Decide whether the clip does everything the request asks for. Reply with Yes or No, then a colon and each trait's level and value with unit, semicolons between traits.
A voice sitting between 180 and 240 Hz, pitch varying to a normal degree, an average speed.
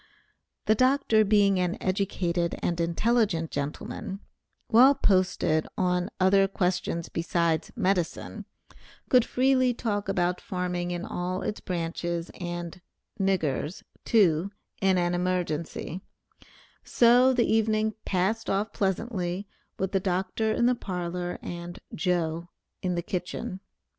No: medium, 185 Hz; average, 3.2 semitones; slow, 120 wpm